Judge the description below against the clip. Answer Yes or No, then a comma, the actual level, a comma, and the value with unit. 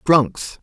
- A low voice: No, medium, 145 Hz